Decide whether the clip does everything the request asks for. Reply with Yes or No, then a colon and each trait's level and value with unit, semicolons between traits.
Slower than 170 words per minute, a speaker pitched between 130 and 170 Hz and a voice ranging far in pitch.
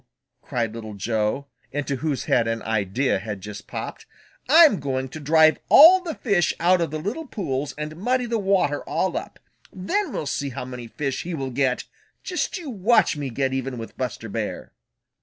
No: average, 185 wpm; medium, 140 Hz; wide, 7.8 semitones